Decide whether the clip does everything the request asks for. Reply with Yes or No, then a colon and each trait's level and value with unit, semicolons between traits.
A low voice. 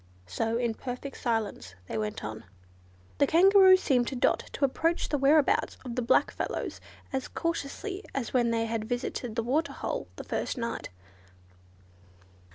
No: very high, 250 Hz